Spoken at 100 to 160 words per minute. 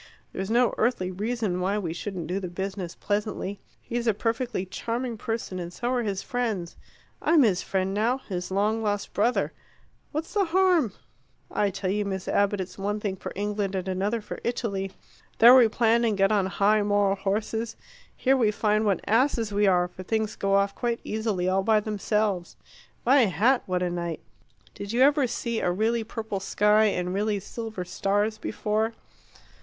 No: average, 180 wpm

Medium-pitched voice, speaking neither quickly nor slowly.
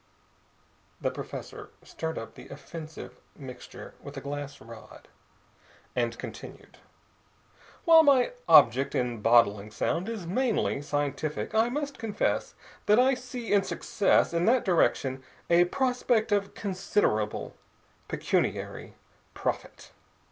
No: medium, 170 Hz; slow, 115 wpm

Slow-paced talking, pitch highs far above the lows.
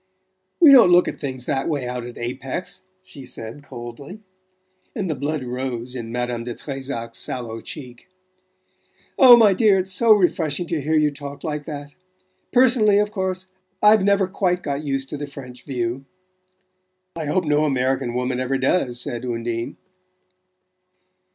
No: average, 160 wpm; wide, 6.6 semitones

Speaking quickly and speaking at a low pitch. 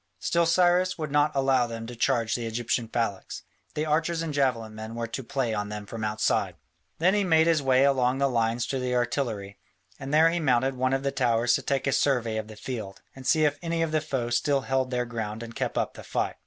Yes: fast, 235 wpm; low, 130 Hz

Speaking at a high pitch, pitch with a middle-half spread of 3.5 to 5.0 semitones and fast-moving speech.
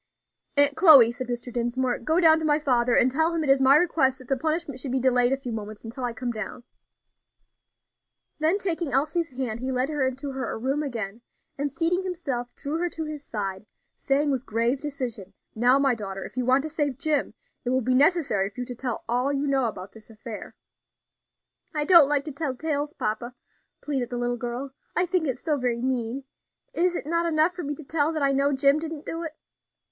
Yes: very high, 270 Hz; average, 3.9 semitones; fast, 215 wpm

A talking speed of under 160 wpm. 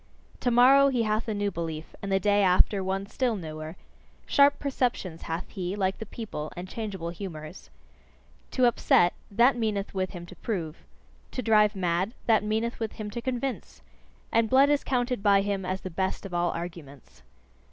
No: average, 175 wpm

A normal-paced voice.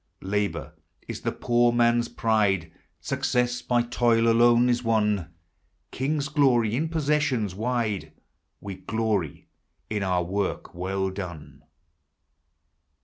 No: slow, 120 wpm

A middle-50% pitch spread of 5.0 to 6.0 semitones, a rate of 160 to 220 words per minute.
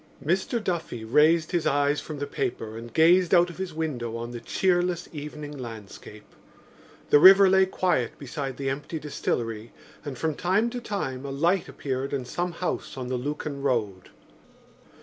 Yes: wide, 5.6 semitones; average, 170 wpm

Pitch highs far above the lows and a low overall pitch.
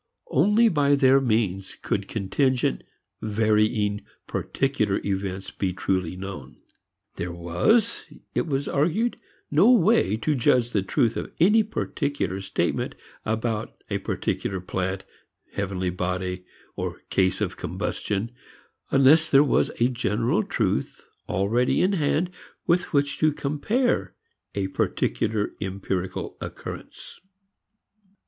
Yes: wide, 7.1 semitones; low, 110 Hz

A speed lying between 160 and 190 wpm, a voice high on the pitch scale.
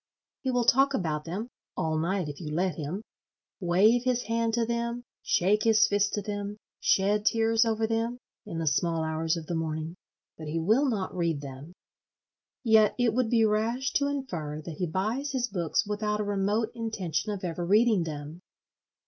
Yes: average, 175 wpm; high, 205 Hz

